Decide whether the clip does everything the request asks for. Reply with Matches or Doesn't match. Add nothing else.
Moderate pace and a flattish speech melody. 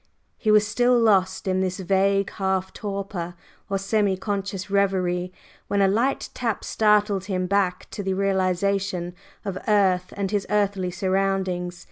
Matches